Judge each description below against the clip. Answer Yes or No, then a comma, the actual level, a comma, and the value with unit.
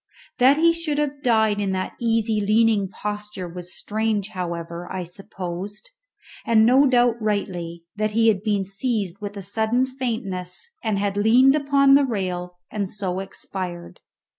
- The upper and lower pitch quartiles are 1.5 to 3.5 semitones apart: No, average, 4.0 semitones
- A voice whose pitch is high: Yes, high, 210 Hz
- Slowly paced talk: No, average, 155 wpm